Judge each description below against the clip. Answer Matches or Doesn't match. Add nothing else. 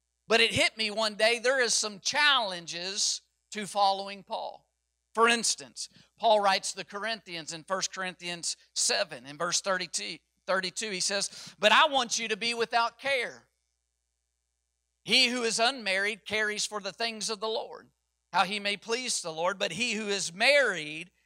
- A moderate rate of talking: Matches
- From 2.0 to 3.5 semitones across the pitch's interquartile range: Doesn't match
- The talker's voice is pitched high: Matches